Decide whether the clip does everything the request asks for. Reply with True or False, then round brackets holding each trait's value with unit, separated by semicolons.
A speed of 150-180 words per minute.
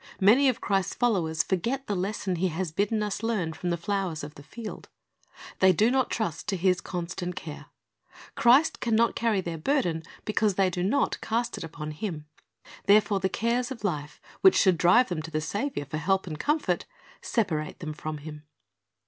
False (190 wpm)